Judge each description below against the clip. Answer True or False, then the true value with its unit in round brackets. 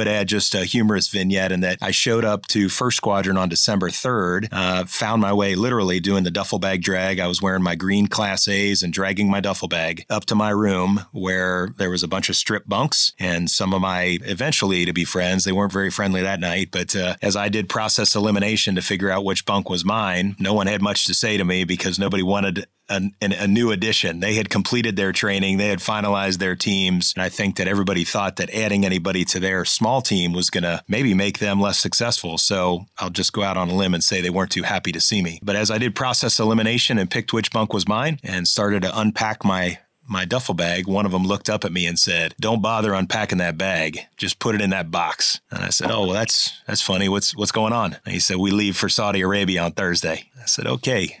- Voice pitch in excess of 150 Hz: False (100 Hz)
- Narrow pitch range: True (2.1 semitones)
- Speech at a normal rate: False (245 wpm)